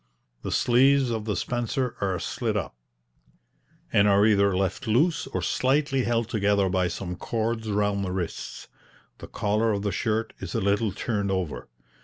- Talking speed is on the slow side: No, average, 165 wpm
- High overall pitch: No, low, 105 Hz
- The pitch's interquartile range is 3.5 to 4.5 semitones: No, average, 3.0 semitones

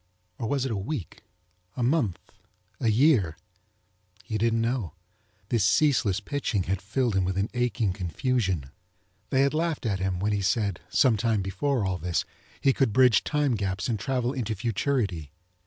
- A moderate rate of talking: Yes, average, 170 wpm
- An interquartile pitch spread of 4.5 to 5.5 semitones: Yes, average, 5.2 semitones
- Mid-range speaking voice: No, low, 110 Hz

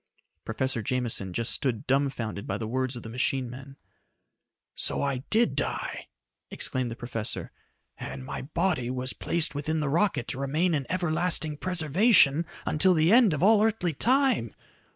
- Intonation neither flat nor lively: No, wide, 5.7 semitones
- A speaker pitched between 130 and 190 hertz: Yes, medium, 140 Hz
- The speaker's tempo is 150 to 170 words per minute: Yes, average, 155 wpm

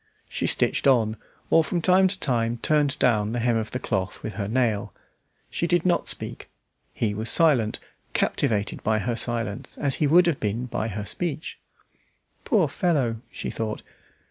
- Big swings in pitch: Yes, wide, 6.1 semitones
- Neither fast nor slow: Yes, average, 170 wpm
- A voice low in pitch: Yes, low, 120 Hz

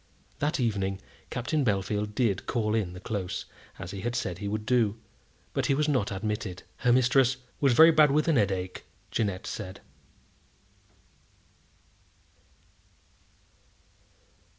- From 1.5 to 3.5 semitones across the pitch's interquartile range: No, average, 4.5 semitones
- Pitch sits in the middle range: No, low, 110 Hz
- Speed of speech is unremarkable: No, slow, 130 wpm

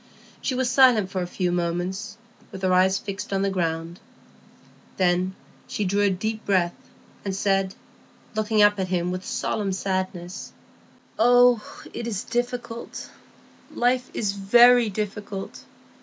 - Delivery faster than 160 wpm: No, slow, 135 wpm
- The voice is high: Yes, high, 195 Hz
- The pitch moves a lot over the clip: No, average, 3.1 semitones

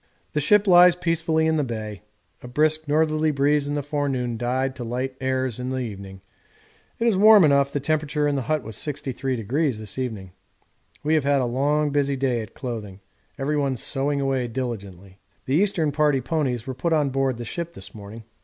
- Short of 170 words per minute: No, average, 190 wpm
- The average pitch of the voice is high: No, low, 135 Hz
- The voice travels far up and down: No, average, 3.8 semitones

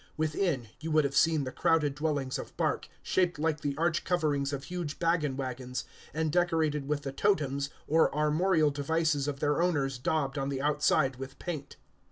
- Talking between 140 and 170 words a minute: No, average, 180 wpm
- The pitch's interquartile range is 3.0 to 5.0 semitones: No, narrow, 2.6 semitones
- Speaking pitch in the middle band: Yes, medium, 150 Hz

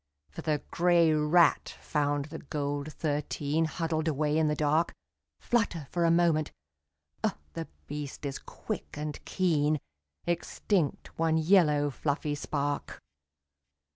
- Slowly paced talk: Yes, slow, 125 wpm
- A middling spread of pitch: No, narrow, 2.1 semitones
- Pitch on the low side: No, medium, 155 Hz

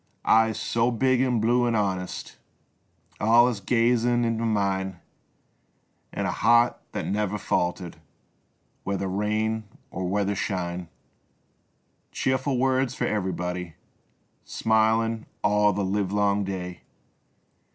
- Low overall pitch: Yes, low, 105 Hz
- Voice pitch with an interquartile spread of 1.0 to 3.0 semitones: No, average, 3.4 semitones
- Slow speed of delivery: Yes, slow, 105 wpm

